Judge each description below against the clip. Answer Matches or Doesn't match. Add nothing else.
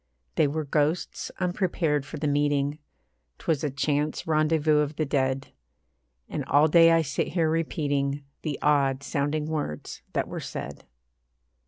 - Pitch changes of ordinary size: Doesn't match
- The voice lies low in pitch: Doesn't match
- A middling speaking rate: Matches